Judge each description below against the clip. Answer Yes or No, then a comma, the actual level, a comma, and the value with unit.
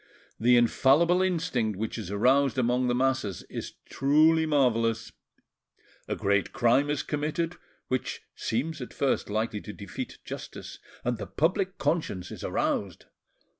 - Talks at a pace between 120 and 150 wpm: Yes, slow, 135 wpm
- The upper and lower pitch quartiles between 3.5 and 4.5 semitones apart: No, wide, 5.4 semitones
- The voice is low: Yes, low, 125 Hz